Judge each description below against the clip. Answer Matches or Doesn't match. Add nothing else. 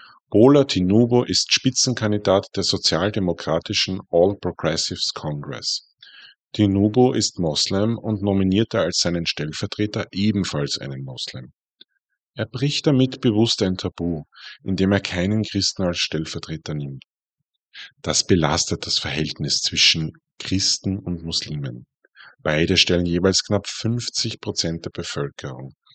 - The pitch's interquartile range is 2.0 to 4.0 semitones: Doesn't match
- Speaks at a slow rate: Matches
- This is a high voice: Doesn't match